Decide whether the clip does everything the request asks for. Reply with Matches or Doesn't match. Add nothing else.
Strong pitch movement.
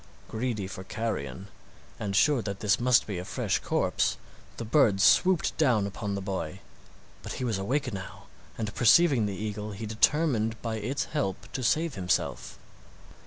Doesn't match